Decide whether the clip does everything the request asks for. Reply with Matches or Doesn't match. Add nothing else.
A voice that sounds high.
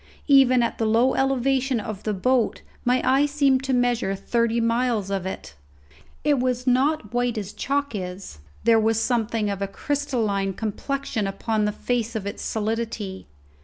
Matches